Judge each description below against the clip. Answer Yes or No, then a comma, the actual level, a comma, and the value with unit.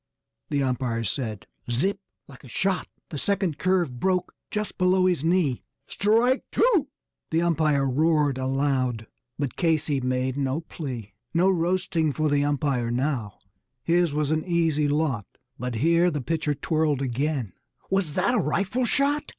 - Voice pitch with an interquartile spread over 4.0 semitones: Yes, average, 5.2 semitones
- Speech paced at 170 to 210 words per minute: No, average, 150 wpm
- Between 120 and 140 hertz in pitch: No, medium, 150 Hz